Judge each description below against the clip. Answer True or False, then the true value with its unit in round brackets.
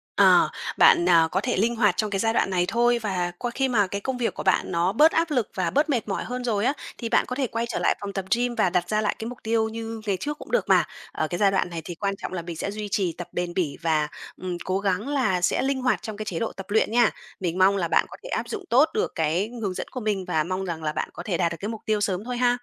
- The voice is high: True (205 Hz)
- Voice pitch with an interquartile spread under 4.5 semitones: False (4.8 semitones)